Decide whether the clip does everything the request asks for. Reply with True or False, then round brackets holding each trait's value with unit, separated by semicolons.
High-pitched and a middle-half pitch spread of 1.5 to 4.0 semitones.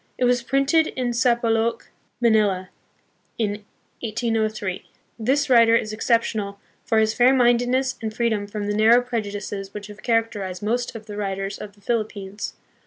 True (220 Hz; 2.8 semitones)